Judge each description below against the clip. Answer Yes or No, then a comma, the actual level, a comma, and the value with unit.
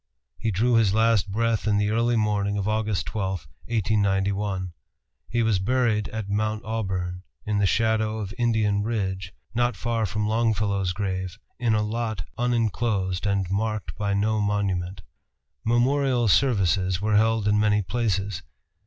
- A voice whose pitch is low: Yes, low, 105 Hz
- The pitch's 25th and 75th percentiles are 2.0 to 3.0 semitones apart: Yes, narrow, 2.4 semitones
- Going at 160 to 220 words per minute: No, average, 145 wpm